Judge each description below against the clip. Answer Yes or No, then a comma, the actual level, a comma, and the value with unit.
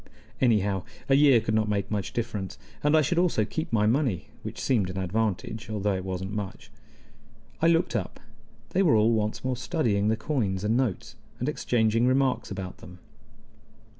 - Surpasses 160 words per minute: Yes, average, 175 wpm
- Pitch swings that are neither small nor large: Yes, average, 4.4 semitones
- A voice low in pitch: Yes, low, 110 Hz